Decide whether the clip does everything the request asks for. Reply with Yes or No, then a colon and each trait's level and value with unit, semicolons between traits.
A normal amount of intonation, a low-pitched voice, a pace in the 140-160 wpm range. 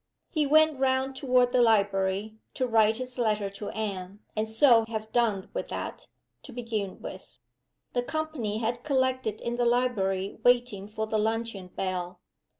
No: average, 3.5 semitones; high, 225 Hz; average, 155 wpm